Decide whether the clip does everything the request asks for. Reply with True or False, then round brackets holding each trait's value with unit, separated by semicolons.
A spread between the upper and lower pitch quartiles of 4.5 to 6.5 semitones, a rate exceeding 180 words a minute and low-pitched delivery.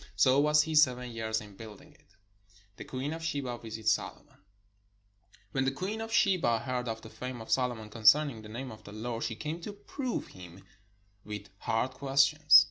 True (5.1 semitones; 190 wpm; 125 Hz)